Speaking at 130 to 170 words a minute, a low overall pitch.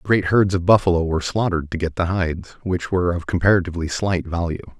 No: average, 200 wpm; very low, 90 Hz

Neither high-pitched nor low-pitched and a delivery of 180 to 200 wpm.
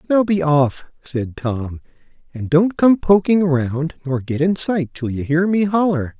Yes: medium, 160 Hz; average, 185 wpm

